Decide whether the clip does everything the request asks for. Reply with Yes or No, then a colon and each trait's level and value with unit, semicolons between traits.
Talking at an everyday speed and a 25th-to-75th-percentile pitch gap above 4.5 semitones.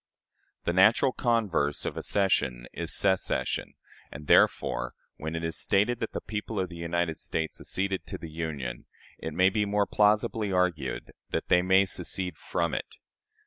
No: average, 155 wpm; average, 4.0 semitones